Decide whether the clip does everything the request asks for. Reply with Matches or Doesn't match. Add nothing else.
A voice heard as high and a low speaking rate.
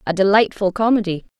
Matches